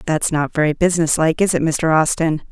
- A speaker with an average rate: No, fast, 215 wpm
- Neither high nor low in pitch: Yes, medium, 160 Hz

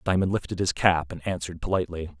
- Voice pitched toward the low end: Yes, very low, 85 Hz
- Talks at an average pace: Yes, average, 190 wpm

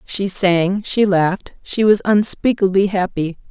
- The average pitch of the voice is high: Yes, high, 195 Hz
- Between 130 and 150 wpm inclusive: Yes, slow, 135 wpm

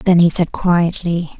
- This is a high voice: No, medium, 170 Hz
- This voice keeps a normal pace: Yes, average, 175 wpm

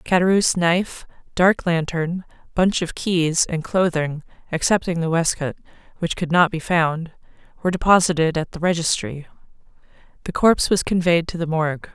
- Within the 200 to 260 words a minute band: No, average, 145 wpm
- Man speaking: No, female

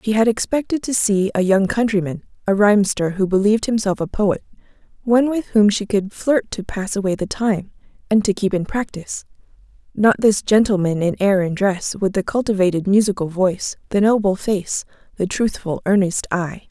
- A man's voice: No, female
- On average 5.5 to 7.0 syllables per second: No, 5.3 syllables/s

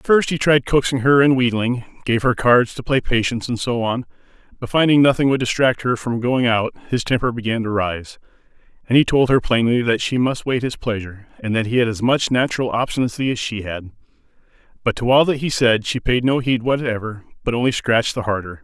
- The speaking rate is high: Yes, fast, 220 wpm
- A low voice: Yes, low, 120 Hz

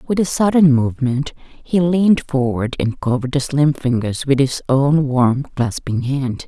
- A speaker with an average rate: Yes, average, 165 wpm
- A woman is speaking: Yes, female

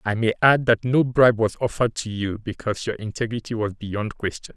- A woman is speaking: No, male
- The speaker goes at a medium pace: No, fast, 210 wpm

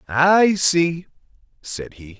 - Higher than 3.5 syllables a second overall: No, 2.7 syllables/s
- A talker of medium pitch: Yes, medium, 155 Hz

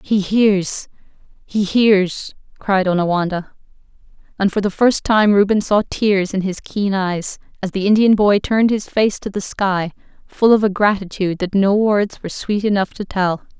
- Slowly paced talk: No, average, 175 wpm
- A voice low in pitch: No, high, 200 Hz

